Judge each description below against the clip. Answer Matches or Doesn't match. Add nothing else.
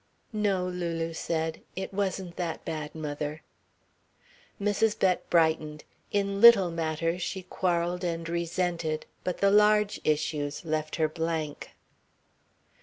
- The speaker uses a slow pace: Matches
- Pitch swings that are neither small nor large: Matches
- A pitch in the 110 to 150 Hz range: Doesn't match